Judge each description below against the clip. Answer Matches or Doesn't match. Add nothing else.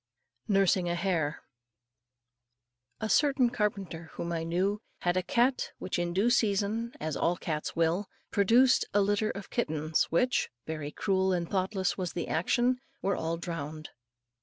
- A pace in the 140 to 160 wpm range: Matches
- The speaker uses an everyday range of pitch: Matches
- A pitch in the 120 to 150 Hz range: Doesn't match